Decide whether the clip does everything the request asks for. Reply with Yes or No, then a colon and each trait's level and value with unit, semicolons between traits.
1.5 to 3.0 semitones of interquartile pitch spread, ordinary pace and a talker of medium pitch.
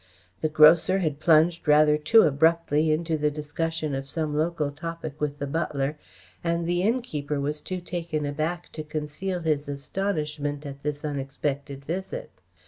Yes: narrow, 2.4 semitones; average, 150 wpm; medium, 155 Hz